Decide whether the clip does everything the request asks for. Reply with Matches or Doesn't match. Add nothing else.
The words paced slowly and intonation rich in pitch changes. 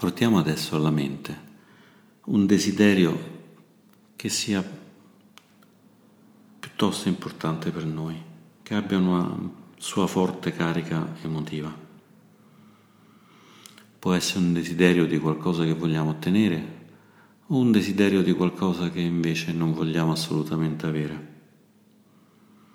Doesn't match